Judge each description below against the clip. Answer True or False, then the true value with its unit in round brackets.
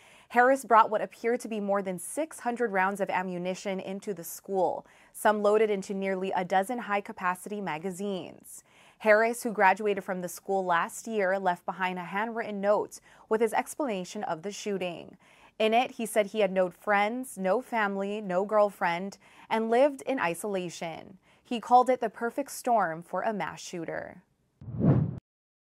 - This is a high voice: True (205 Hz)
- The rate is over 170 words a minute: False (160 wpm)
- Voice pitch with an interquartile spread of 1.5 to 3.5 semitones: True (3.1 semitones)